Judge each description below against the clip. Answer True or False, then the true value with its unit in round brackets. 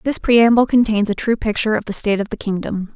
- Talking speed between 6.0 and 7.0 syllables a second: True (6.4 syllables/s)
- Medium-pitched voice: False (215 Hz)